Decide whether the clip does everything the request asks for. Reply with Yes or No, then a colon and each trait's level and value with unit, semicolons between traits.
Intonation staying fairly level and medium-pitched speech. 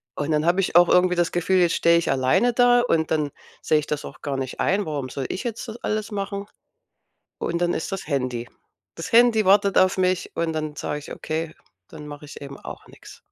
No: average, 4.8 semitones; medium, 170 Hz